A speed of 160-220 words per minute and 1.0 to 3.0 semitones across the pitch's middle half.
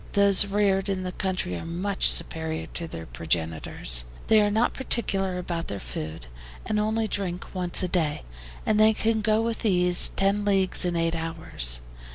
No: average, 175 wpm; average, 4.2 semitones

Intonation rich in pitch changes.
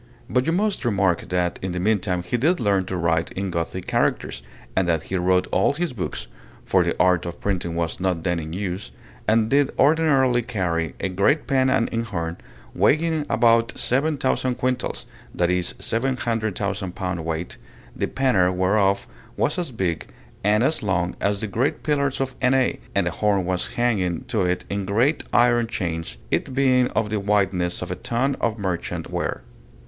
Yes: wide, 5.7 semitones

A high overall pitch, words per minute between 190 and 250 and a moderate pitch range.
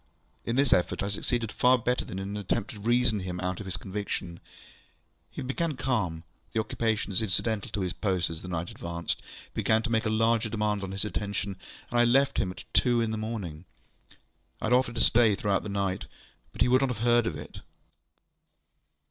No: low, 105 Hz; average, 200 wpm; average, 3.8 semitones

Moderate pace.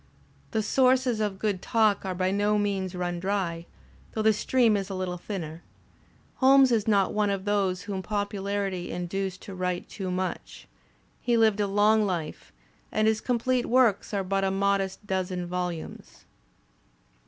Yes: average, 165 wpm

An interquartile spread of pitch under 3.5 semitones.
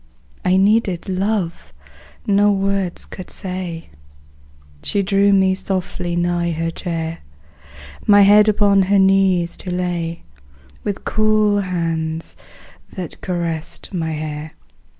Yes: average, 2.8 semitones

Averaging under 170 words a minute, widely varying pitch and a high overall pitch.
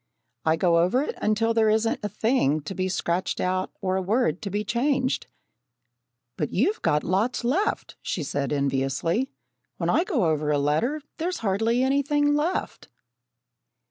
Yes: average, 160 wpm; wide, 7.6 semitones; high, 210 Hz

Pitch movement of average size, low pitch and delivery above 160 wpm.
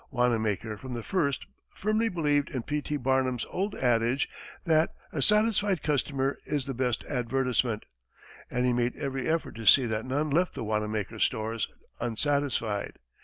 No: average, 4.1 semitones; low, 130 Hz; average, 155 wpm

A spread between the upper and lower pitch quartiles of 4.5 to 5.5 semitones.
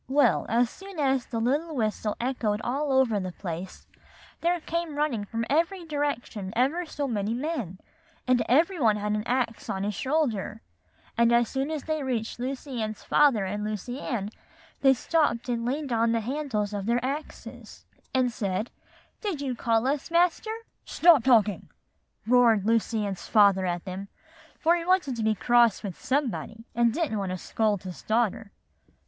Yes: average, 5.2 semitones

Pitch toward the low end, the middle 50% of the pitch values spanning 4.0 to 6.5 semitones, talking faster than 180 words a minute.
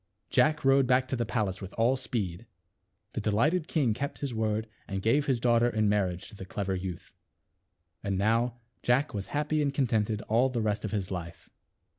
Yes: low, 115 Hz; average, 4.3 semitones; average, 190 wpm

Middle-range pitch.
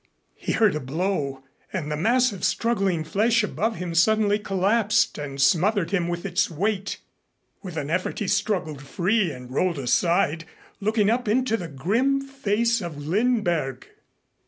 No: high, 195 Hz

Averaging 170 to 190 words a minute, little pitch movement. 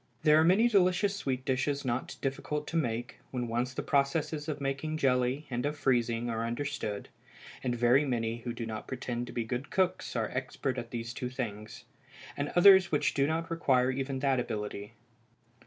No: average, 185 wpm; average, 3.7 semitones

